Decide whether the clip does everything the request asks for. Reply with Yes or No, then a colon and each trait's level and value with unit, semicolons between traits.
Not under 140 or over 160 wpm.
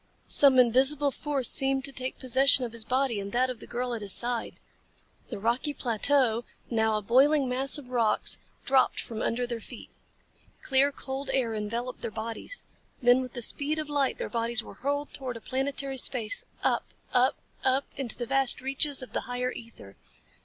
No: average, 180 wpm